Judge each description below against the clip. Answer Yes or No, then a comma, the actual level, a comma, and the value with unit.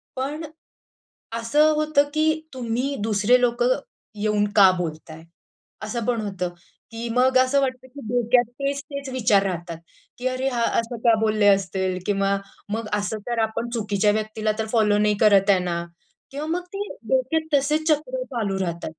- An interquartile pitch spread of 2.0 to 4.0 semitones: No, average, 4.5 semitones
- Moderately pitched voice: No, high, 230 Hz